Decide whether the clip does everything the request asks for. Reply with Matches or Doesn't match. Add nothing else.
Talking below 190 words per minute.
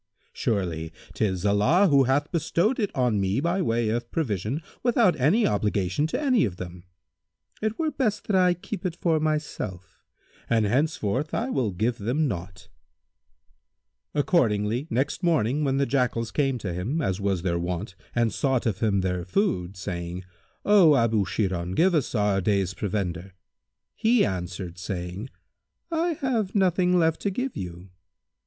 Matches